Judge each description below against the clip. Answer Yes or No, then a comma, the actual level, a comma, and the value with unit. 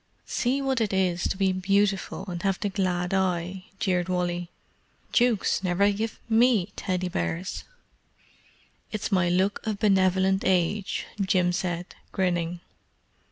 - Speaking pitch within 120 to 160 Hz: No, high, 190 Hz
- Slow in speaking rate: Yes, slow, 130 wpm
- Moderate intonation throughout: No, narrow, 2.2 semitones